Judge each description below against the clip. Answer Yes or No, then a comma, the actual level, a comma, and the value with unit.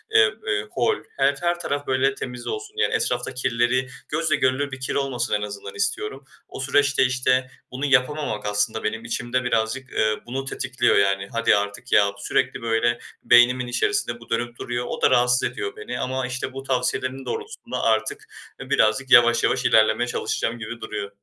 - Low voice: Yes, low, 125 Hz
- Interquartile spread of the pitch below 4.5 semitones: Yes, narrow, 2.6 semitones